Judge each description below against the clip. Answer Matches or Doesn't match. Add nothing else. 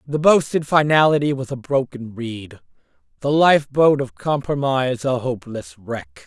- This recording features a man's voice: Matches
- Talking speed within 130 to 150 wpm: Matches